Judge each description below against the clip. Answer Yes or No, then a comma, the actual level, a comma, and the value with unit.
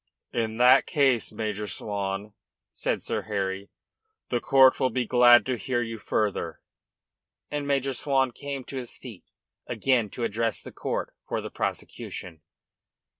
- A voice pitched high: No, low, 120 Hz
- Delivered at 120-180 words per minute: Yes, average, 145 wpm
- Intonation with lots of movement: No, average, 3.8 semitones